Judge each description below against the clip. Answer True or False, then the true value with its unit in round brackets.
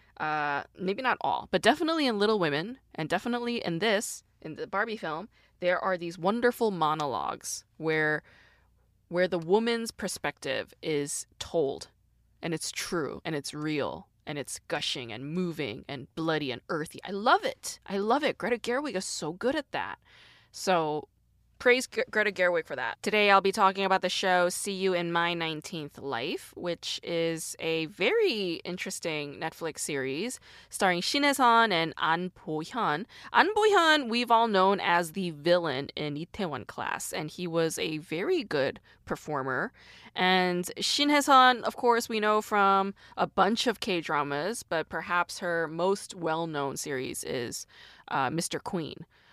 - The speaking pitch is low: False (180 Hz)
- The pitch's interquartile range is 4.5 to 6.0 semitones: True (5.4 semitones)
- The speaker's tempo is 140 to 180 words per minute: True (160 wpm)